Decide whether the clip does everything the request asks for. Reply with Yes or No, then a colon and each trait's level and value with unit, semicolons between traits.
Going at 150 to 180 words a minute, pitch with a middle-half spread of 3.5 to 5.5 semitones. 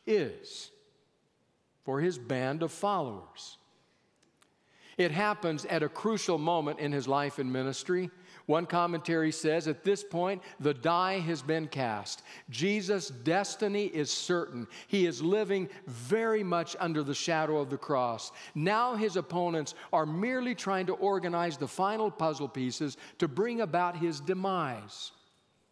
No: average, 140 wpm; average, 4.7 semitones